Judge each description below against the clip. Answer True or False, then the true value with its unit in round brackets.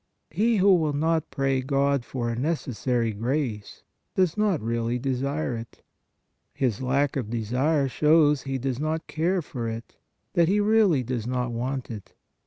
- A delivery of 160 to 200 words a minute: True (170 wpm)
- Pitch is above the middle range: False (135 Hz)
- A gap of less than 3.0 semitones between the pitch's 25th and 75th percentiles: False (4.7 semitones)